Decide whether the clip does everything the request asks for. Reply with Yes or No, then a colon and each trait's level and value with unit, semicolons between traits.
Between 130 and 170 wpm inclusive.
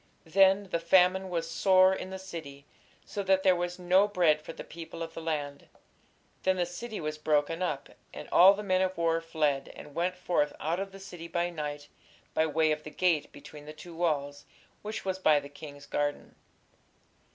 No: average, 195 wpm